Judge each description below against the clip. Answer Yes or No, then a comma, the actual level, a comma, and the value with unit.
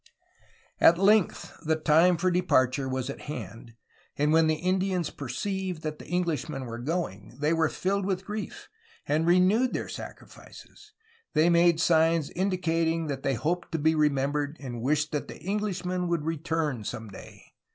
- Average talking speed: Yes, average, 160 wpm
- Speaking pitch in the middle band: Yes, medium, 160 Hz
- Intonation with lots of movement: No, average, 3.8 semitones